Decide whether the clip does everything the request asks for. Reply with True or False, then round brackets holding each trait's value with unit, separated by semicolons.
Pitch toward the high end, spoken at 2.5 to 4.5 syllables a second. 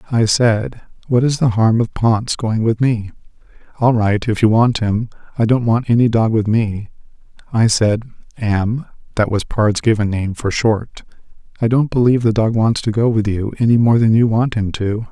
False (115 Hz; 4.4 syllables/s)